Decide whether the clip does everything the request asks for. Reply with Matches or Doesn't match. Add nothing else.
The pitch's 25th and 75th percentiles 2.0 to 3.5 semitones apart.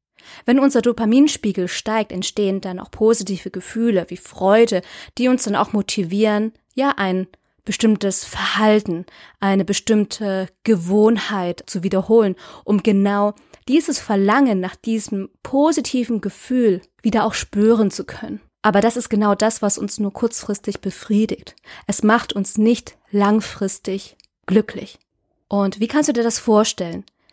Matches